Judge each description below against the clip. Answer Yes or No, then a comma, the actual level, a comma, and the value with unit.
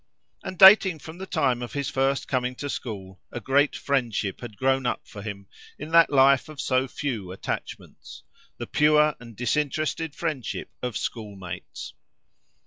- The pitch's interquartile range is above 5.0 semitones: No, average, 4.5 semitones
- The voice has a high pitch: No, low, 135 Hz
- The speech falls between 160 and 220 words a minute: No, average, 150 wpm